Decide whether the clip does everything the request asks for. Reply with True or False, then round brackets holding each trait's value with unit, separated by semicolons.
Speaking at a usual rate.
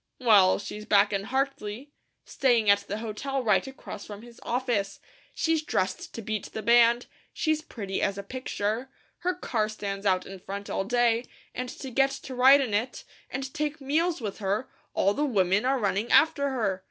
True (185 wpm)